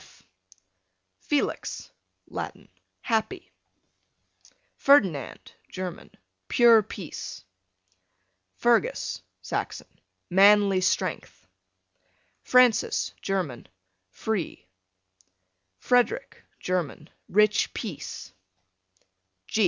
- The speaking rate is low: Yes, slow, 60 wpm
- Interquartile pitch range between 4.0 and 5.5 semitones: Yes, average, 4.8 semitones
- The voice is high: Yes, high, 205 Hz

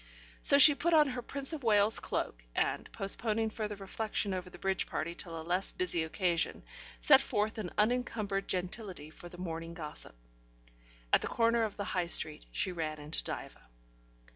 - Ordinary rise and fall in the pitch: Yes, average, 4.7 semitones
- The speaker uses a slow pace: No, average, 175 wpm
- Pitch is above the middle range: Yes, high, 195 Hz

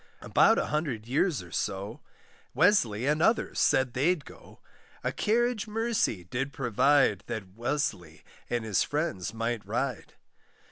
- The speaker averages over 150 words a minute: No, slow, 135 wpm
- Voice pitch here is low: Yes, low, 125 Hz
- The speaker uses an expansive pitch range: Yes, wide, 6.3 semitones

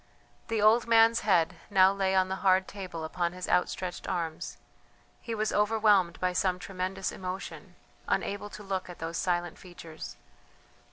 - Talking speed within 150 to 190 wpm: Yes, average, 155 wpm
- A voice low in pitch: No, medium, 185 Hz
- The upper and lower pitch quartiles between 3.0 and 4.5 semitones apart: No, narrow, 2.5 semitones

